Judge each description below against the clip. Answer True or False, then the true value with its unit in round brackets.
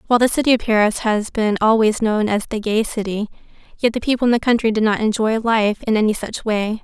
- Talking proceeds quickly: True (235 wpm)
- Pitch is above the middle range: True (220 Hz)